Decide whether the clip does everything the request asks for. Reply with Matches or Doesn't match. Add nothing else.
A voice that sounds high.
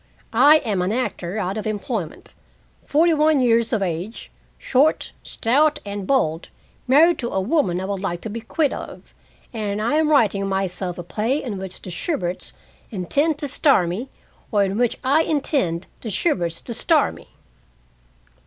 Matches